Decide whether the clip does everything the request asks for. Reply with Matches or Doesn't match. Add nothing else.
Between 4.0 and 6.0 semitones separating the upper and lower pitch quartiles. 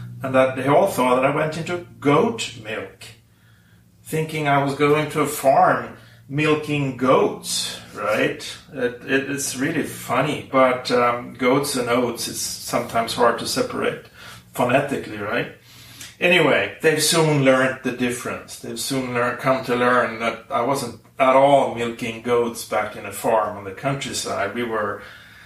Doesn't match